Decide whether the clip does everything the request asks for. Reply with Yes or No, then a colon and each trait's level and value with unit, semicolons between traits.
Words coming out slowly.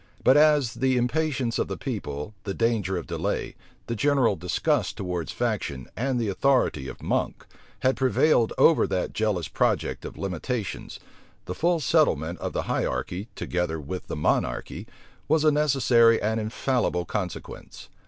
No: average, 150 wpm